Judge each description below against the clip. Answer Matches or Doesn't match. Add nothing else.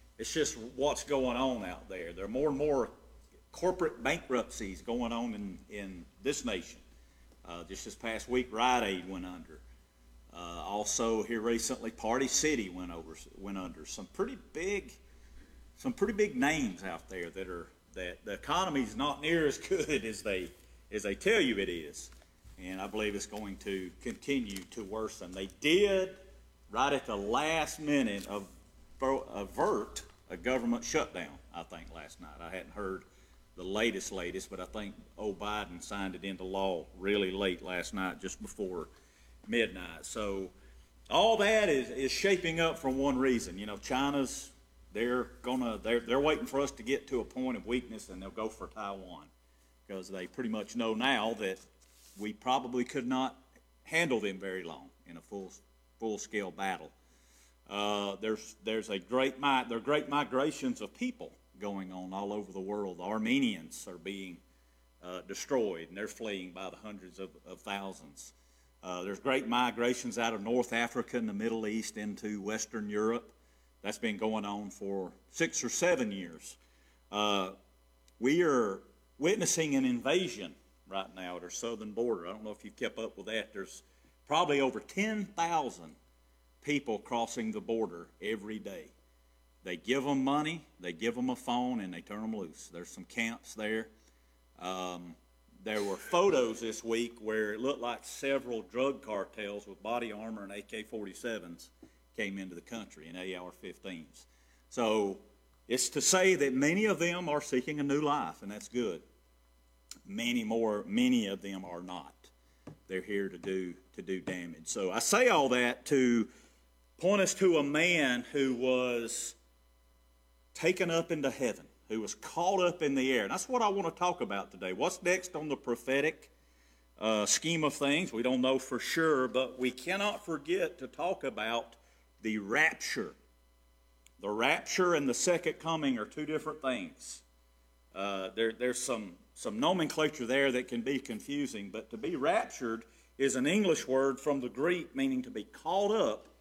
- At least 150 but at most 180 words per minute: Matches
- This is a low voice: Matches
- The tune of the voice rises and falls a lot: Matches